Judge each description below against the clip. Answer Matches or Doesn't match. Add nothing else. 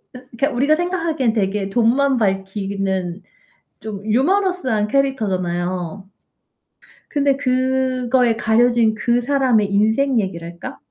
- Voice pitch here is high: Matches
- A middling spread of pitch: Matches